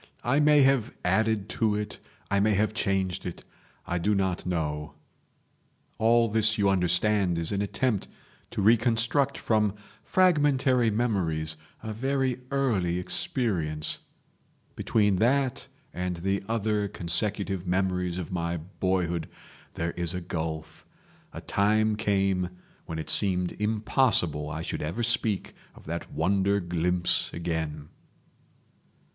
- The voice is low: Yes, low, 100 Hz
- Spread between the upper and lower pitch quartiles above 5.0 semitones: No, average, 4.2 semitones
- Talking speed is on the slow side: Yes, slow, 125 wpm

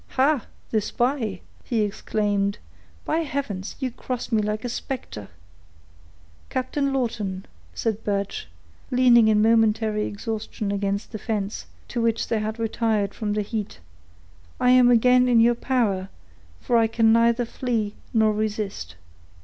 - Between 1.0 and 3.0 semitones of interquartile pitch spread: Yes, average, 2.7 semitones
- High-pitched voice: Yes, high, 225 Hz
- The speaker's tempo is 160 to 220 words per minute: No, average, 140 wpm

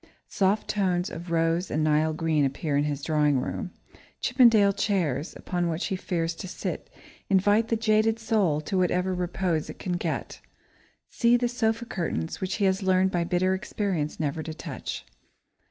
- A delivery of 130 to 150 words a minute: No, average, 170 wpm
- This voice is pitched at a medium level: Yes, medium, 180 Hz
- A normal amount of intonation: Yes, average, 4.1 semitones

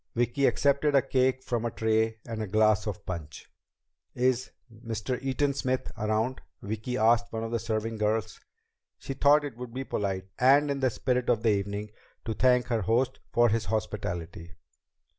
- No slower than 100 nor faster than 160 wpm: No, average, 175 wpm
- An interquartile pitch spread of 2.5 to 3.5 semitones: Yes, average, 3.1 semitones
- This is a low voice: Yes, low, 115 Hz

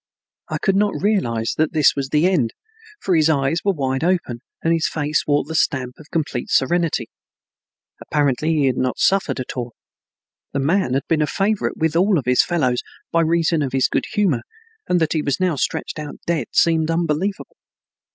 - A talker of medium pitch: Yes, medium, 155 Hz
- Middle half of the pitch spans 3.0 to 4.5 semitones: Yes, average, 4.1 semitones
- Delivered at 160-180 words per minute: No, average, 190 wpm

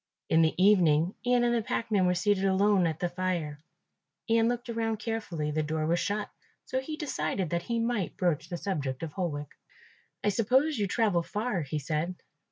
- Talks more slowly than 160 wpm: No, average, 185 wpm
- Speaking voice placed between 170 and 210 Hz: Yes, high, 190 Hz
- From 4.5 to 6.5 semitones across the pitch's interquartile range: Yes, wide, 5.5 semitones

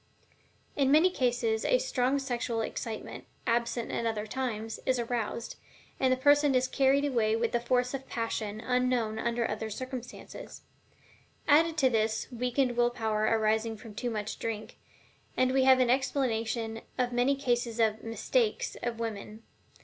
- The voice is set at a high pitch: Yes, high, 240 Hz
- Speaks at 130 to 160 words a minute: Yes, average, 155 wpm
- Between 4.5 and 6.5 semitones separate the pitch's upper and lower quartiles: No, narrow, 2.6 semitones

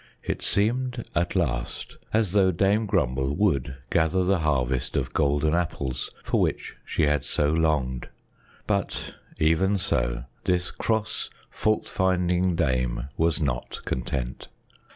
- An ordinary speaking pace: No, slow, 130 wpm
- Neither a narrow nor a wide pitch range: No, wide, 5.9 semitones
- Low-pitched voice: Yes, very low, 80 Hz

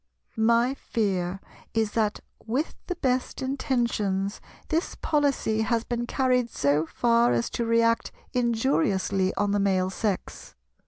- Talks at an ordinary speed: No, slow, 125 wpm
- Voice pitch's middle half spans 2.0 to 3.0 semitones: No, average, 4.2 semitones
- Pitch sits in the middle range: No, high, 230 Hz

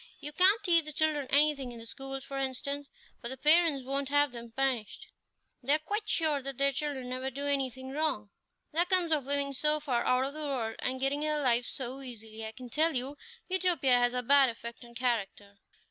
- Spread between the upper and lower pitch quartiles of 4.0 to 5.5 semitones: No, average, 3.2 semitones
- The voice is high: Yes, very high, 275 Hz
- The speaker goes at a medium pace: No, fast, 210 wpm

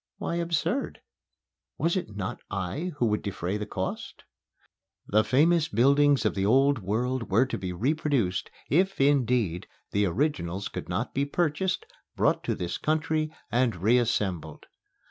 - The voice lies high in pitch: No, low, 120 Hz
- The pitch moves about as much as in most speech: No, wide, 7.1 semitones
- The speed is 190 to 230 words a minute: No, average, 145 wpm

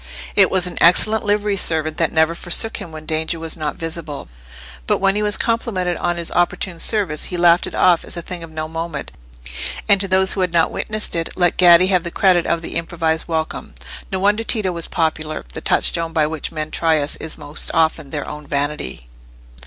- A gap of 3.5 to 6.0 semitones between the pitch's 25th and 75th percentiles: No, average, 2.8 semitones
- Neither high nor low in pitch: Yes, medium, 170 Hz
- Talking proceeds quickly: Yes, fast, 210 wpm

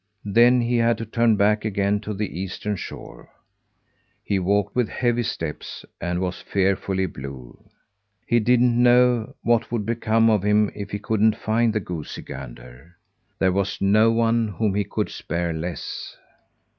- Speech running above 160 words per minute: No, average, 155 wpm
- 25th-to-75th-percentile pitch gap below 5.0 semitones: Yes, average, 3.5 semitones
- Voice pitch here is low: Yes, low, 105 Hz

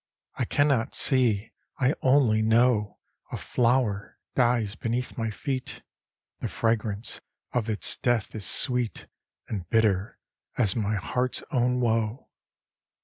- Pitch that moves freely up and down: No, average, 2.8 semitones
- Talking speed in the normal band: No, slow, 125 wpm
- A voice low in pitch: Yes, low, 115 Hz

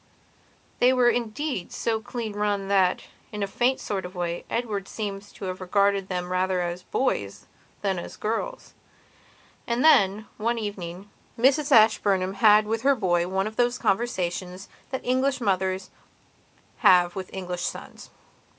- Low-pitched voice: No, high, 200 Hz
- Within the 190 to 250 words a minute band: No, average, 150 wpm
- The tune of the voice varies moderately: Yes, average, 3.9 semitones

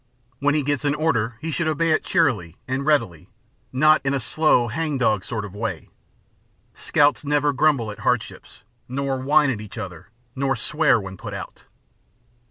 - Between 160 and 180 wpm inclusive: Yes, average, 175 wpm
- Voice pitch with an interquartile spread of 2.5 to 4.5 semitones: No, average, 5.0 semitones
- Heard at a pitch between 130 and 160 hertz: Yes, low, 135 Hz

